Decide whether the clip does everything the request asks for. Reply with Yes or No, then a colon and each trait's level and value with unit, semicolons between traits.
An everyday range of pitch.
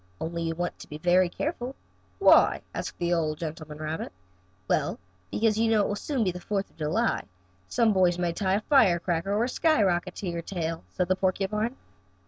Yes: average, 4.1 semitones